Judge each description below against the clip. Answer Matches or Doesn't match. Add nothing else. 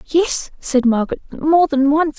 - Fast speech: Doesn't match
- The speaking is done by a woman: Matches